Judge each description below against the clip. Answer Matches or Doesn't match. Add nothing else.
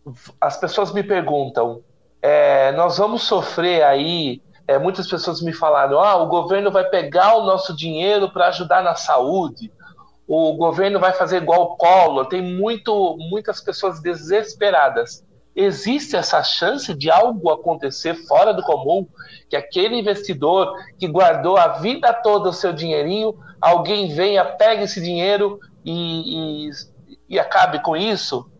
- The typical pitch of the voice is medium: Matches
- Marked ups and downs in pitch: Doesn't match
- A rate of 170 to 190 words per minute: Doesn't match